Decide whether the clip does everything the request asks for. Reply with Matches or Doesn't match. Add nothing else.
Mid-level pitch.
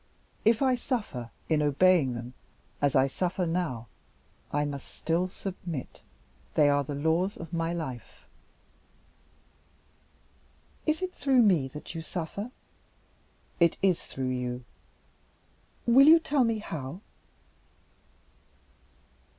Matches